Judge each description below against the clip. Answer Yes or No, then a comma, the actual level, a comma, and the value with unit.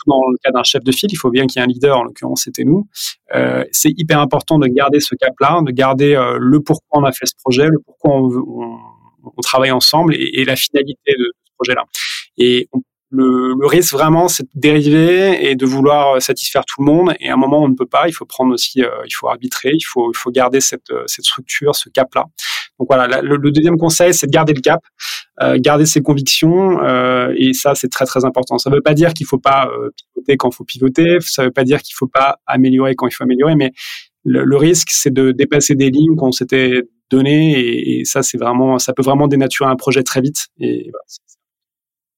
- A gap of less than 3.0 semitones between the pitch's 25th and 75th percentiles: Yes, narrow, 2.6 semitones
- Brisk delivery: Yes, fast, 250 wpm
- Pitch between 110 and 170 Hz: Yes, low, 135 Hz